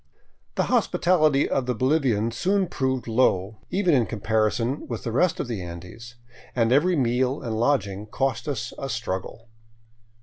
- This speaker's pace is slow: No, average, 155 wpm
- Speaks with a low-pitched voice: Yes, low, 120 Hz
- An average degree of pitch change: Yes, average, 3.9 semitones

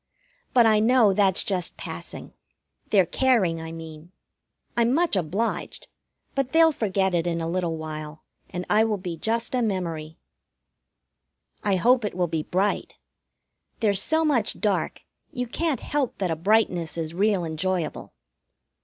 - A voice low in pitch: No, high, 190 Hz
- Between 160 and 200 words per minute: No, average, 150 wpm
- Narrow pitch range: No, wide, 5.5 semitones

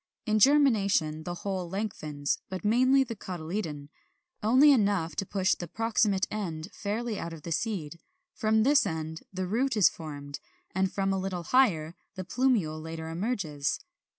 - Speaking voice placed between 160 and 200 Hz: Yes, high, 190 Hz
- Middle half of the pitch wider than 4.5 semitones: Yes, average, 5.2 semitones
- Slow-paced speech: No, average, 155 wpm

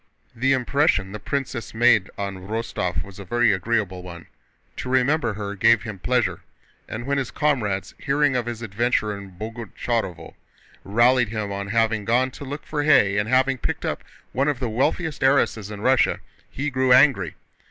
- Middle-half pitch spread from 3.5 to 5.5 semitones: Yes, average, 4.4 semitones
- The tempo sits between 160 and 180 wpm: Yes, average, 175 wpm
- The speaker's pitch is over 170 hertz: No, low, 115 Hz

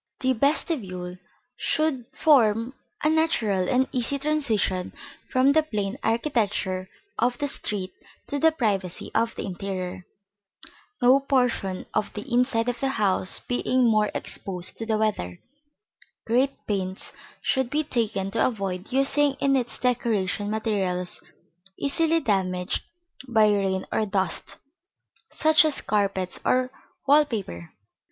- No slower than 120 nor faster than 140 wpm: Yes, slow, 135 wpm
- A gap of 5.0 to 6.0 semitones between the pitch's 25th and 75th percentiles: Yes, wide, 5.5 semitones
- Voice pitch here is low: No, high, 225 Hz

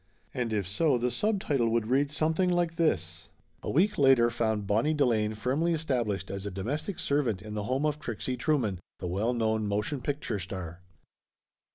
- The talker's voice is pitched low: Yes, low, 120 Hz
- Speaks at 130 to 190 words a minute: Yes, average, 175 wpm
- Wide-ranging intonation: Yes, wide, 6.2 semitones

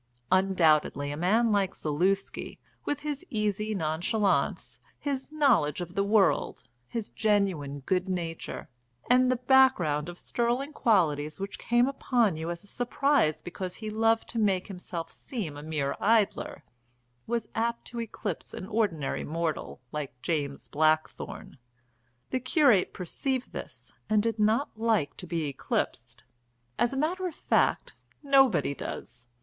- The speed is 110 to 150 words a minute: Yes, average, 140 wpm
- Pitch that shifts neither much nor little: No, wide, 6.6 semitones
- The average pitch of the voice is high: Yes, high, 200 Hz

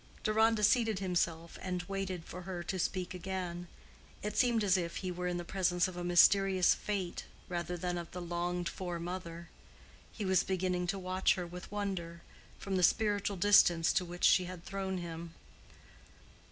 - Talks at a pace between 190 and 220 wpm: No, average, 175 wpm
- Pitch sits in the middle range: Yes, medium, 180 Hz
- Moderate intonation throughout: No, narrow, 1.8 semitones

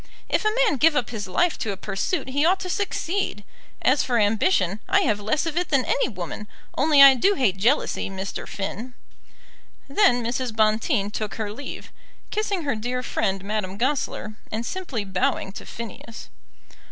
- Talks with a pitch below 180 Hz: No, high, 240 Hz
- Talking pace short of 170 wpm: No, average, 175 wpm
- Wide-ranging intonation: Yes, wide, 6.7 semitones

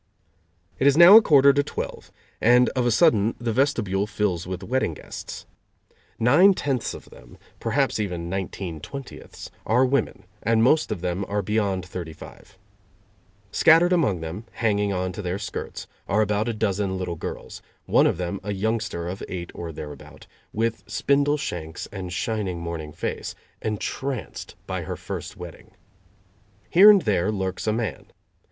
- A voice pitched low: Yes, low, 105 Hz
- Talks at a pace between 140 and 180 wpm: Yes, average, 160 wpm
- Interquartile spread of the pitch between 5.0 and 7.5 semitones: Yes, average, 5.3 semitones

